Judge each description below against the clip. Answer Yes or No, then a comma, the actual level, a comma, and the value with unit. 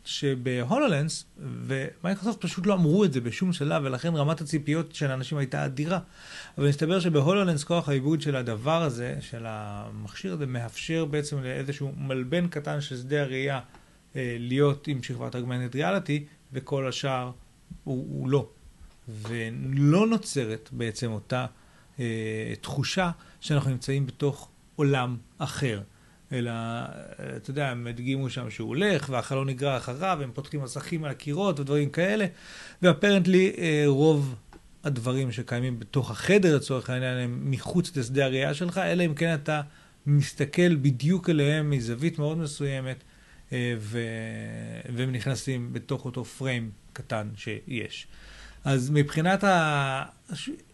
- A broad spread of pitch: No, average, 4.2 semitones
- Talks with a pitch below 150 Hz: Yes, medium, 140 Hz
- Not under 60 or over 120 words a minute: No, average, 130 wpm